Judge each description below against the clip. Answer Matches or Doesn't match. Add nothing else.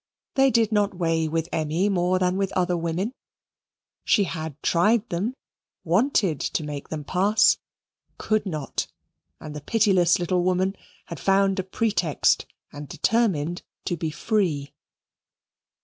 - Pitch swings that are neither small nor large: Matches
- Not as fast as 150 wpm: Matches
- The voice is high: Doesn't match